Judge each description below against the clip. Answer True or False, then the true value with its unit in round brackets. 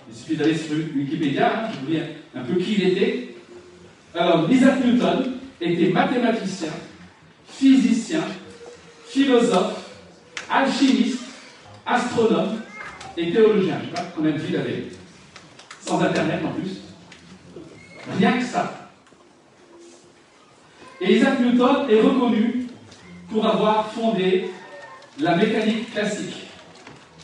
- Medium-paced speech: False (115 wpm)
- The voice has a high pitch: True (220 Hz)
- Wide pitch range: True (6.2 semitones)